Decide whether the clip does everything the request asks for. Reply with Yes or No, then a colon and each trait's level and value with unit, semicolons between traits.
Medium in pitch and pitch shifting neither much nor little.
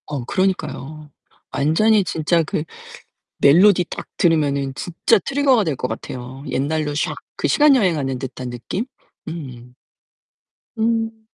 No: medium, 155 Hz; wide, 6.7 semitones